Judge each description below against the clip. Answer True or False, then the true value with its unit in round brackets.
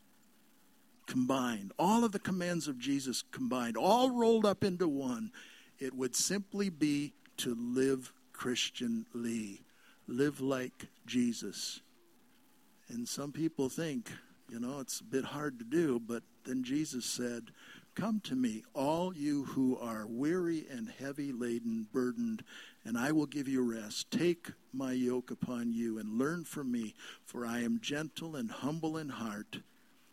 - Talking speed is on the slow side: False (145 wpm)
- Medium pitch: True (145 Hz)